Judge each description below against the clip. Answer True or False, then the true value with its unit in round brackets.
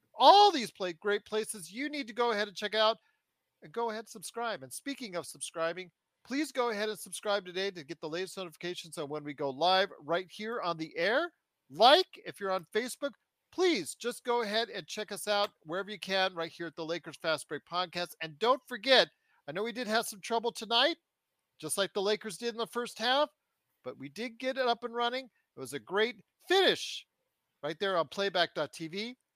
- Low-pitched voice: False (205 Hz)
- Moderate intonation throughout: False (5.8 semitones)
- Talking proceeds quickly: True (210 wpm)